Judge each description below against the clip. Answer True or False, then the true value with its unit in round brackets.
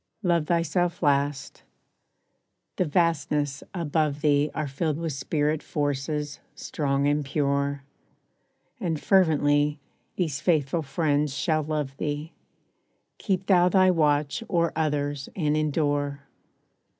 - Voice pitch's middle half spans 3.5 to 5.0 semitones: False (2.4 semitones)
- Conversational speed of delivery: False (110 wpm)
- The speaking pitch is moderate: True (150 Hz)